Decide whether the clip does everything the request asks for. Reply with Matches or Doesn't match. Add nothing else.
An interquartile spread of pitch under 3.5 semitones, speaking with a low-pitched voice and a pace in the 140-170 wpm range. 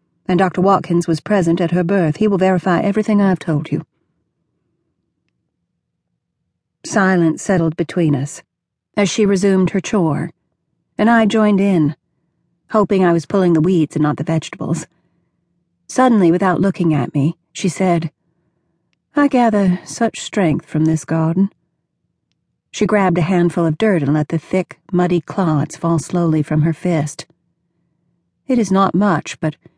Doesn't match